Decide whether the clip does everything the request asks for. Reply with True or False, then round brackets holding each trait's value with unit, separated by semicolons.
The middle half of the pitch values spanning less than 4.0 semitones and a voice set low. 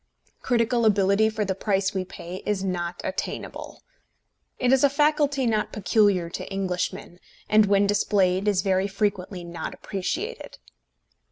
False (2.6 semitones; 200 Hz)